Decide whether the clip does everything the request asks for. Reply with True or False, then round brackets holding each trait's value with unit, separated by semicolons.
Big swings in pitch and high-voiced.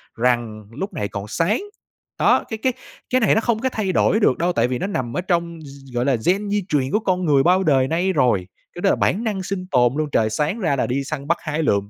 False (7.1 semitones; 160 Hz)